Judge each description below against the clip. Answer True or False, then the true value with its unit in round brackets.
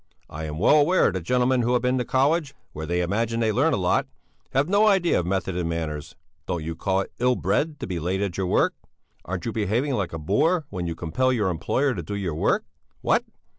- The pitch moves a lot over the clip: True (6.9 semitones)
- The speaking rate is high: True (235 wpm)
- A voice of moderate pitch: False (100 Hz)